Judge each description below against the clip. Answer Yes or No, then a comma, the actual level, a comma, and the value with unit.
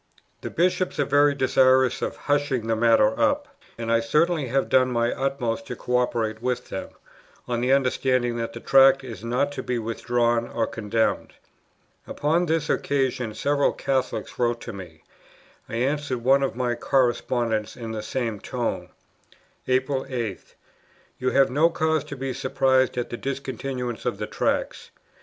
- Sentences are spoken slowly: No, average, 160 wpm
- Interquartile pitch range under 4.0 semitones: Yes, average, 2.8 semitones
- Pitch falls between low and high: No, low, 125 Hz